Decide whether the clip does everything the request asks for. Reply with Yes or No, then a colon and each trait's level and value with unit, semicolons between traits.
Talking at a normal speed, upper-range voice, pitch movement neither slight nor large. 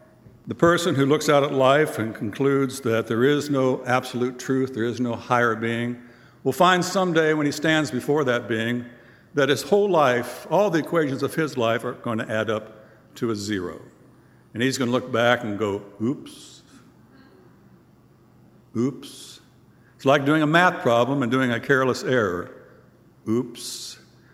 No: average, 170 wpm; low, 125 Hz; average, 3.3 semitones